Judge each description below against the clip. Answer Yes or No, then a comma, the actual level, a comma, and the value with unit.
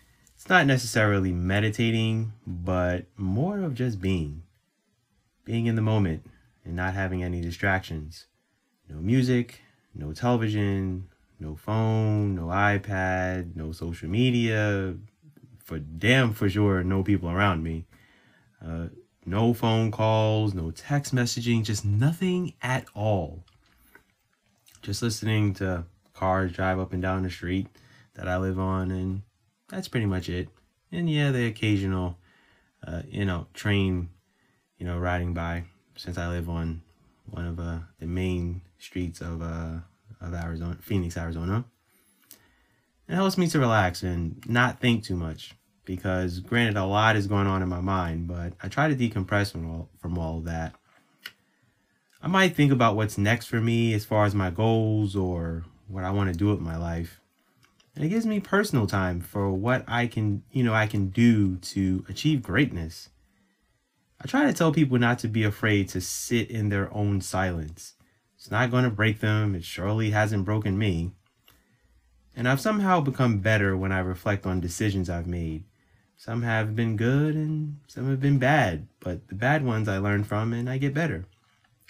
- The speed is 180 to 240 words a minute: No, average, 165 wpm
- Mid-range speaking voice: No, low, 100 Hz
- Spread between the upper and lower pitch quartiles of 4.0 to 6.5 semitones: Yes, average, 4.3 semitones